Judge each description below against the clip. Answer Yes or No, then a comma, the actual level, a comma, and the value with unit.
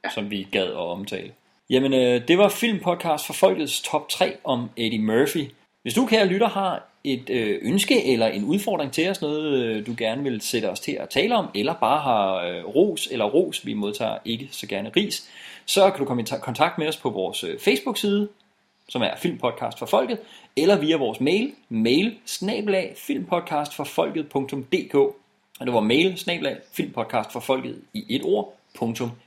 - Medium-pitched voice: Yes, medium, 155 Hz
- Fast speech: No, average, 165 wpm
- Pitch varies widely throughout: Yes, wide, 8.5 semitones